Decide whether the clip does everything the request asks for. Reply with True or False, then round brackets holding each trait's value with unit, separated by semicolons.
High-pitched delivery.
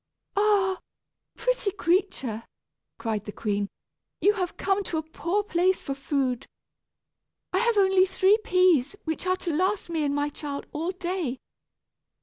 True (360 Hz)